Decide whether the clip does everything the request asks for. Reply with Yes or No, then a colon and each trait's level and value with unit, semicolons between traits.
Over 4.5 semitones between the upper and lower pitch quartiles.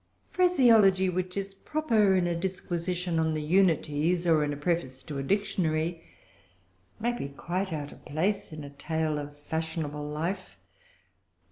No: average, 3.8 semitones